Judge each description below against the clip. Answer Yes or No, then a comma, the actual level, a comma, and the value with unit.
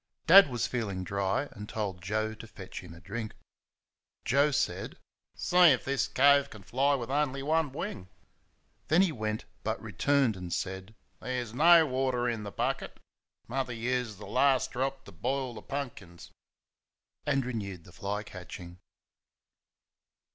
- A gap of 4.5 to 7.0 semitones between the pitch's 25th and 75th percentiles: Yes, wide, 5.5 semitones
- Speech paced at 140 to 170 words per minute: Yes, average, 155 wpm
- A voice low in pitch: Yes, low, 120 Hz